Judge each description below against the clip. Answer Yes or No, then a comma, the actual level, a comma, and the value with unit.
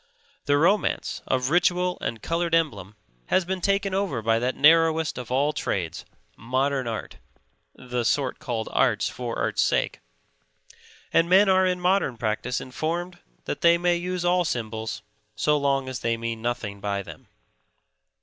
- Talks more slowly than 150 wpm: No, average, 155 wpm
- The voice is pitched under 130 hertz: No, medium, 140 Hz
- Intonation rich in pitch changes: Yes, wide, 6.9 semitones